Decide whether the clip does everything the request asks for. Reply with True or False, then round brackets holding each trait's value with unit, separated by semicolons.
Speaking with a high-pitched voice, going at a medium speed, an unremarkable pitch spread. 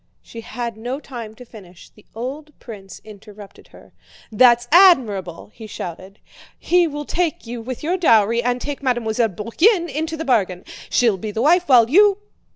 False (240 Hz; 165 wpm; 5.8 semitones)